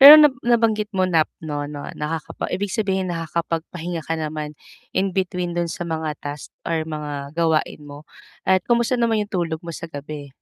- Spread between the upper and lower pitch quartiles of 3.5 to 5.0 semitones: Yes, average, 3.8 semitones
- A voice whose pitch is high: No, medium, 165 Hz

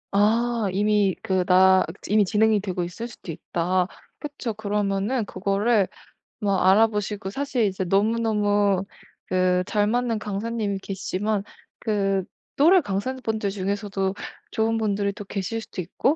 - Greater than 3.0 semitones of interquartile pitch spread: No, narrow, 2.5 semitones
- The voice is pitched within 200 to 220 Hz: Yes, high, 205 Hz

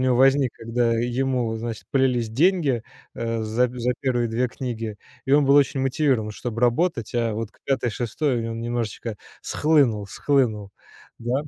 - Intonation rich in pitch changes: No, average, 2.8 semitones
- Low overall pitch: Yes, low, 120 Hz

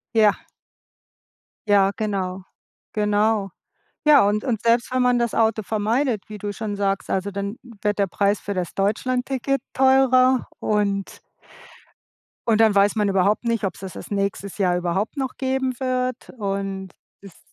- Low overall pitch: No, high, 210 Hz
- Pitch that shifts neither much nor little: Yes, average, 3.6 semitones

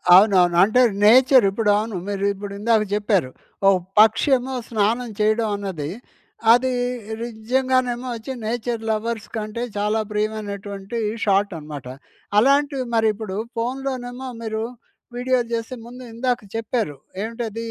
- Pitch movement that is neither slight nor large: Yes, average, 3.1 semitones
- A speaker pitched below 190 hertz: No, high, 225 Hz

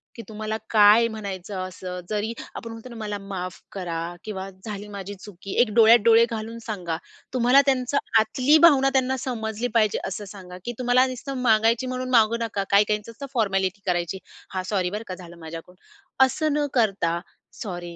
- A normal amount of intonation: Yes, average, 3.7 semitones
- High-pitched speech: Yes, high, 215 Hz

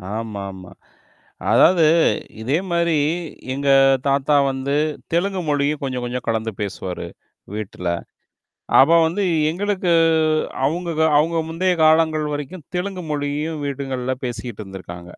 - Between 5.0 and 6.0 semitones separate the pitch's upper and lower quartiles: Yes, wide, 5.4 semitones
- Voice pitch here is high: No, medium, 145 Hz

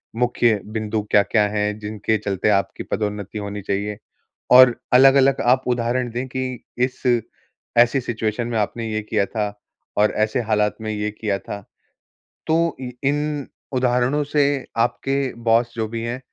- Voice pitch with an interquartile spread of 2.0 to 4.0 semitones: Yes, average, 3.2 semitones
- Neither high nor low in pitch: No, low, 115 Hz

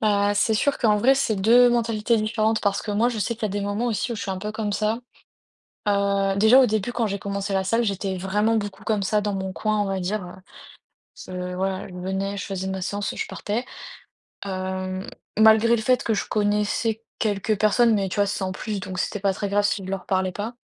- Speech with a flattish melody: Yes, narrow, 2.1 semitones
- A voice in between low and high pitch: No, high, 205 Hz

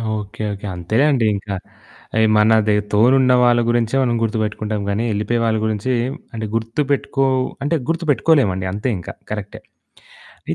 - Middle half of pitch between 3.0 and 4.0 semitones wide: Yes, average, 3.5 semitones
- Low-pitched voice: Yes, low, 110 Hz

